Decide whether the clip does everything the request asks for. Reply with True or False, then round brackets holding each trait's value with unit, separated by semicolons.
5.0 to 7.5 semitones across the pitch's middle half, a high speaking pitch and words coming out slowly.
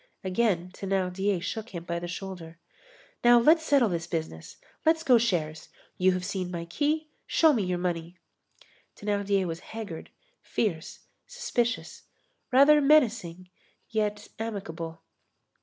True (5.5 semitones; 195 Hz; 125 wpm)